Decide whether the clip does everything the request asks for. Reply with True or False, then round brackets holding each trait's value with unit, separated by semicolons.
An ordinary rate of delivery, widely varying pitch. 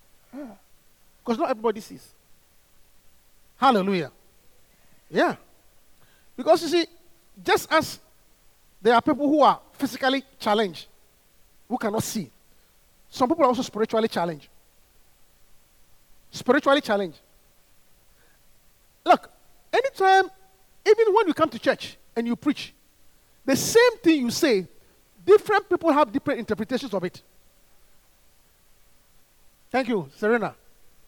False (105 wpm; 6.4 semitones)